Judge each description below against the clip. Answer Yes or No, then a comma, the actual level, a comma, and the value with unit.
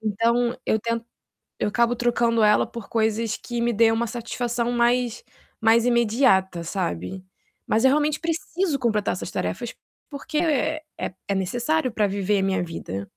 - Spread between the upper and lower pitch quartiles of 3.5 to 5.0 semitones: No, average, 2.8 semitones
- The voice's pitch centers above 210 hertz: Yes, high, 235 Hz